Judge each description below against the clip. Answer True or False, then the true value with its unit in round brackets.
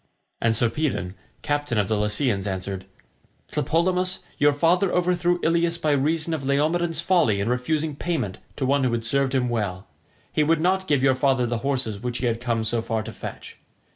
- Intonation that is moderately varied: False (6.2 semitones)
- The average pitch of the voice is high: False (135 Hz)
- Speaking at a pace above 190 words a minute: False (185 wpm)